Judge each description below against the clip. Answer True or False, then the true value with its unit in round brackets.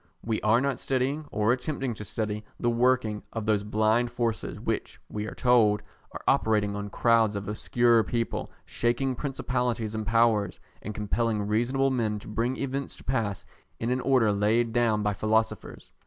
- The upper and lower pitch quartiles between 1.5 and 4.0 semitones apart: True (2.6 semitones)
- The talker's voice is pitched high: False (115 Hz)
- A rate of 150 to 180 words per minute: True (170 wpm)